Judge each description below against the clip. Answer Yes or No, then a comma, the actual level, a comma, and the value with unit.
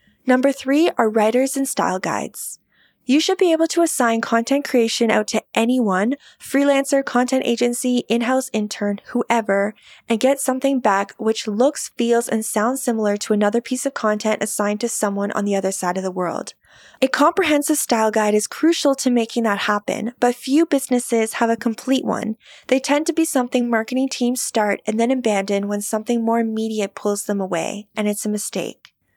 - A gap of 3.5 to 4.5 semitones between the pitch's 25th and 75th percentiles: Yes, average, 3.8 semitones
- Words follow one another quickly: No, average, 180 wpm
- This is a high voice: Yes, high, 235 Hz